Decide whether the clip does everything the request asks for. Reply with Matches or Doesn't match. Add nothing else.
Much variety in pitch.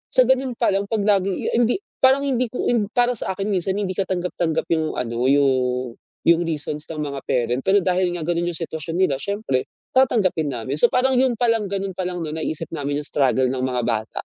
Matches